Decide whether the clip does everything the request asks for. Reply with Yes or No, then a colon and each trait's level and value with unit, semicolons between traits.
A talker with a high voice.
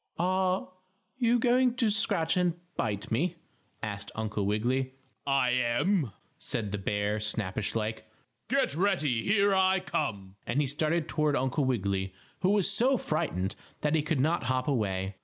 No: low, 135 Hz